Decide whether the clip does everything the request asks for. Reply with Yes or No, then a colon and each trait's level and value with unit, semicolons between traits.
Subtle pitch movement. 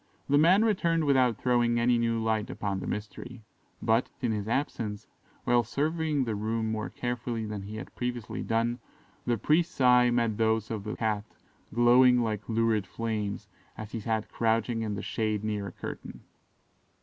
Yes: narrow, 2.2 semitones